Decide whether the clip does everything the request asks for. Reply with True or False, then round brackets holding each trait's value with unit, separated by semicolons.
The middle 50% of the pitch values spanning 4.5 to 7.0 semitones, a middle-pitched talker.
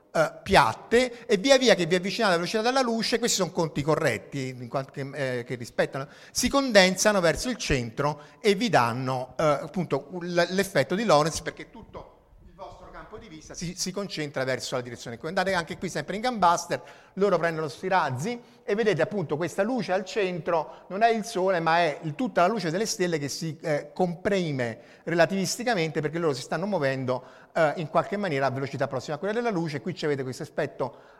True (5.0 semitones; 170 Hz)